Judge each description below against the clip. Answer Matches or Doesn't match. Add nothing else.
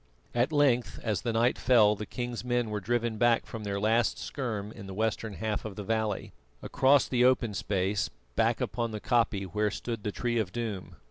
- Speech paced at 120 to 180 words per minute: Doesn't match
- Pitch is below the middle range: Matches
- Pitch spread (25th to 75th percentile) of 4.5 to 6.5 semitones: Doesn't match